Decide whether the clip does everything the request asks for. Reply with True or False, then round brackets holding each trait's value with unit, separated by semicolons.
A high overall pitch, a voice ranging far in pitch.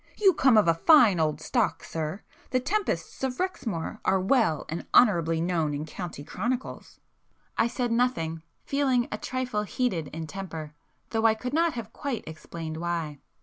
True (205 Hz; 7.5 semitones)